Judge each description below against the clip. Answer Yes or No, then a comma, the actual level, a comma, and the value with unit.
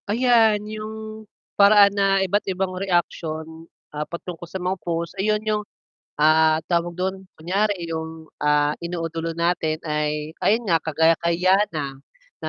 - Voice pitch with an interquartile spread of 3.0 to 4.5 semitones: Yes, average, 3.9 semitones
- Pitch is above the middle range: No, medium, 175 Hz